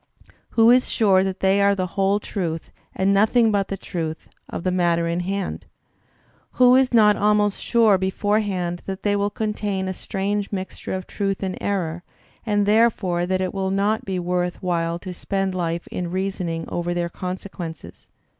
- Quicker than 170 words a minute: Yes, average, 180 wpm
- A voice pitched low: No, high, 190 Hz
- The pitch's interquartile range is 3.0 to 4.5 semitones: No, narrow, 2.4 semitones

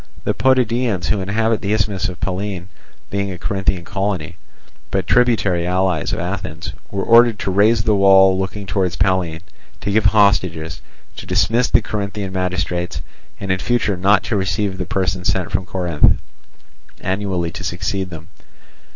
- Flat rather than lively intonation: Yes, narrow, 2.2 semitones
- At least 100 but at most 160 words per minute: Yes, average, 155 wpm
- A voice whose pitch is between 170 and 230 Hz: No, very low, 95 Hz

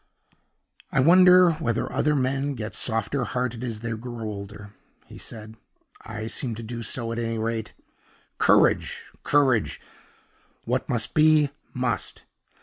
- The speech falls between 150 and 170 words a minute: No, slow, 135 wpm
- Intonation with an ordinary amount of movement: Yes, average, 3.5 semitones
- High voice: No, low, 115 Hz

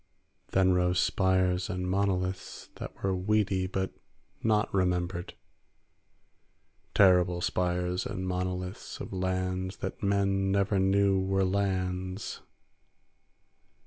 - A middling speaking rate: No, slow, 100 wpm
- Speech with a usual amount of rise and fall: No, narrow, 1.0 semitones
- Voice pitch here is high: No, very low, 95 Hz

